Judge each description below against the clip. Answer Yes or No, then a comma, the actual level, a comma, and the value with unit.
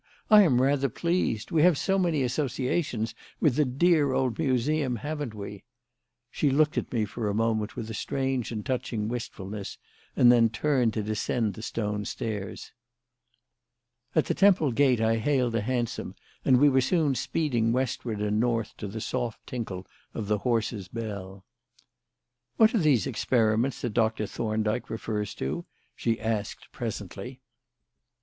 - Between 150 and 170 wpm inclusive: Yes, average, 155 wpm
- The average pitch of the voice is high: No, low, 120 Hz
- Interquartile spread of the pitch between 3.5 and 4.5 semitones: Yes, average, 4.0 semitones